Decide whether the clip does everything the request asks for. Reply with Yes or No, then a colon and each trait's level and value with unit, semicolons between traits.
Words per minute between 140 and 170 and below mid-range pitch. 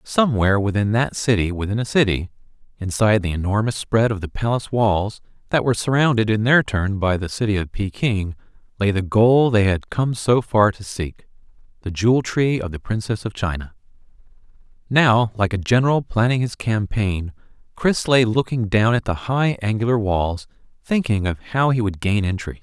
No: average, 180 wpm; low, 110 Hz